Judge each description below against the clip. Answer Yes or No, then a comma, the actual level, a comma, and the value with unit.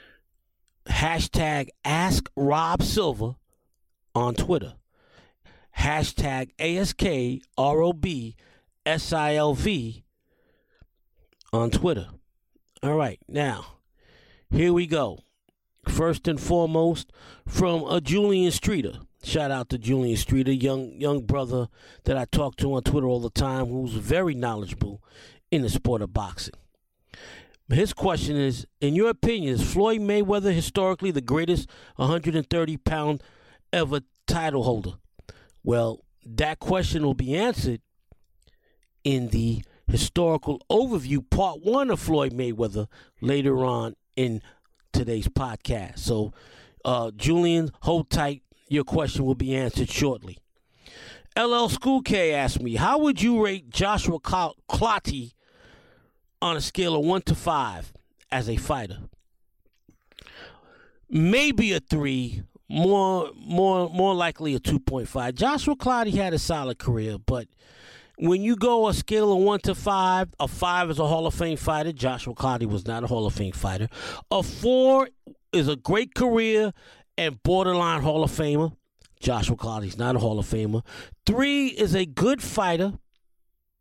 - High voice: No, medium, 145 Hz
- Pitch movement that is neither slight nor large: No, wide, 6.7 semitones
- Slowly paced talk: Yes, slow, 130 wpm